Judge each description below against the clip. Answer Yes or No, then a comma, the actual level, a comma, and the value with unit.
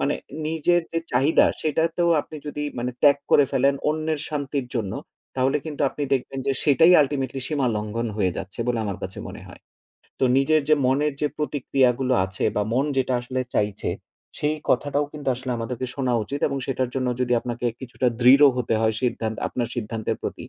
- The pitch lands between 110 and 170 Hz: Yes, low, 135 Hz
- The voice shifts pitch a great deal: No, average, 3.3 semitones